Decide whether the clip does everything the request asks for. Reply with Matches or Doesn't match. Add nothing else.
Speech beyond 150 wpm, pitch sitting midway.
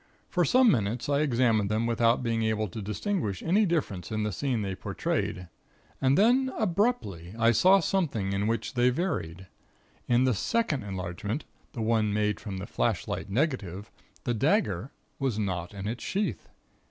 Doesn't match